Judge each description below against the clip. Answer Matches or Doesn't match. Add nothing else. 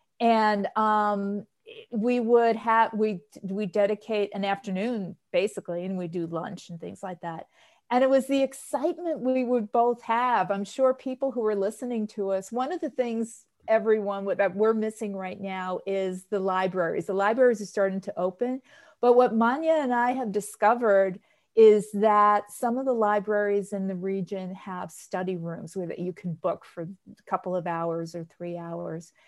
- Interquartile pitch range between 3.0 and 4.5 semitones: Matches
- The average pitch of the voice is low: Doesn't match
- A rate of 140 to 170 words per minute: Doesn't match